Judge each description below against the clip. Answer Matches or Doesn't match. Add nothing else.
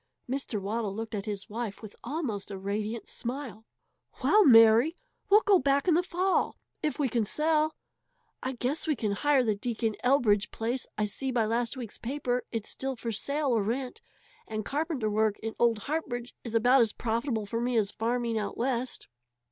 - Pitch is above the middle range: Matches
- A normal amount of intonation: Matches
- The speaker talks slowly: Doesn't match